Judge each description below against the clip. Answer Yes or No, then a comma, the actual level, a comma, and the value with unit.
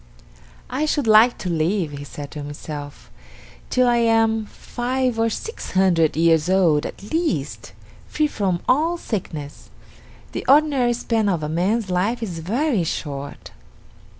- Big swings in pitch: Yes, wide, 7.1 semitones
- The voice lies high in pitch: Yes, high, 200 Hz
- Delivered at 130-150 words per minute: Yes, average, 145 wpm